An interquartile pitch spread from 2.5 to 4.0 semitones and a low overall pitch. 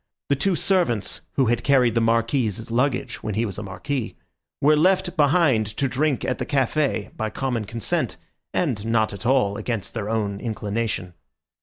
No: average, 4.4 semitones; low, 115 Hz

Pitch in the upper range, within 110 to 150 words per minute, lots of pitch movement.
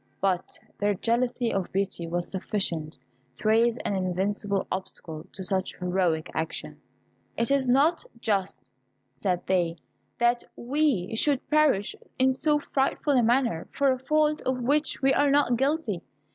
Yes: high, 225 Hz; average, 145 wpm; wide, 6.4 semitones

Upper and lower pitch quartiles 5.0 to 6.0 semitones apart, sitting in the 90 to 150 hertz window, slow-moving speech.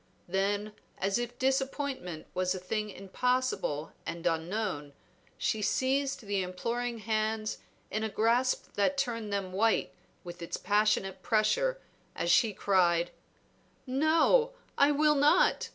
No: average, 5.3 semitones; high, 215 Hz; slow, 125 wpm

